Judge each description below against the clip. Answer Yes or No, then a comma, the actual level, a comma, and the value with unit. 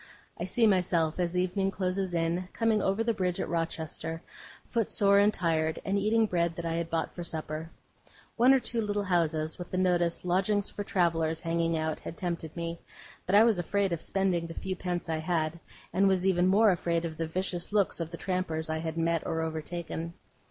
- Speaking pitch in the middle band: Yes, medium, 175 Hz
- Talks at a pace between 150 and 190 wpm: No, average, 200 wpm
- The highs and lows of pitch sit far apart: No, average, 2.7 semitones